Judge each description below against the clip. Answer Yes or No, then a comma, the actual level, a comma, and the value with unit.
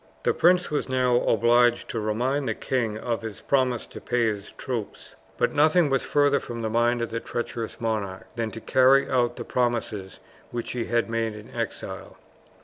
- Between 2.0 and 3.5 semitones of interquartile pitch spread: Yes, narrow, 2.5 semitones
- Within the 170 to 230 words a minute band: Yes, average, 185 wpm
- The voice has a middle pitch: No, low, 120 Hz